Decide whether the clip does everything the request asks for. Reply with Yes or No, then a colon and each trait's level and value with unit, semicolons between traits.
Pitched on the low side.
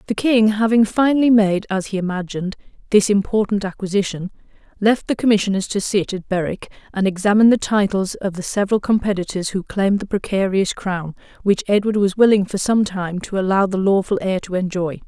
No: high, 200 Hz